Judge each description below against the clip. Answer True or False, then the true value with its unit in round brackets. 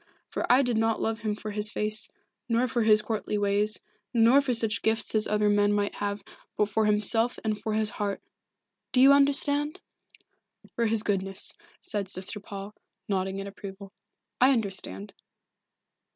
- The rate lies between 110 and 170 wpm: True (165 wpm)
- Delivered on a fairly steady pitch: True (2.0 semitones)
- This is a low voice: False (215 Hz)